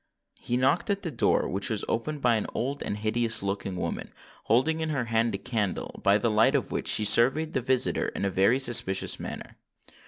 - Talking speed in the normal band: No, fast, 210 wpm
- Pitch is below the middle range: Yes, low, 115 Hz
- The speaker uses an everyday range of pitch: Yes, average, 3.9 semitones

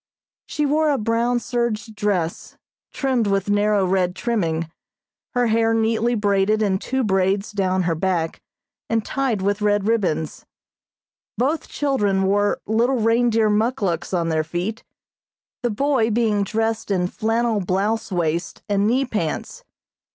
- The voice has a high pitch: Yes, high, 210 Hz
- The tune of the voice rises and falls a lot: No, average, 3.3 semitones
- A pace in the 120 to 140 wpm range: Yes, slow, 135 wpm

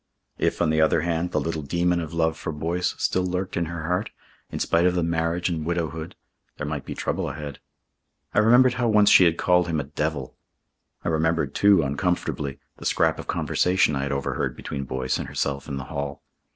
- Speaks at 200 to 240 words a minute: Yes, fast, 205 wpm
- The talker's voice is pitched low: Yes, very low, 80 Hz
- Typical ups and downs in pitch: Yes, average, 3.2 semitones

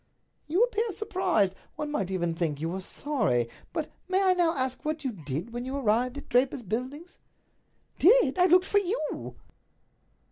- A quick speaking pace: No, average, 175 wpm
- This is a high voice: Yes, very high, 270 Hz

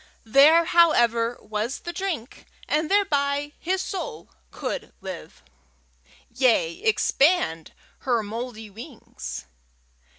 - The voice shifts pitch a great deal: Yes, wide, 7.1 semitones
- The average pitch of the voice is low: No, very high, 275 Hz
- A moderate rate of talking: No, slow, 95 wpm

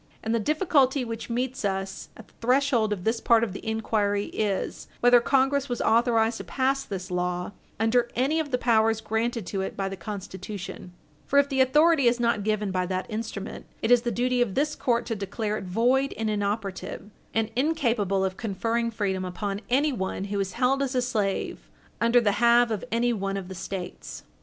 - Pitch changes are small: No, average, 3.8 semitones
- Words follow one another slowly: No, average, 195 wpm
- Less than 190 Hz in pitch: No, high, 225 Hz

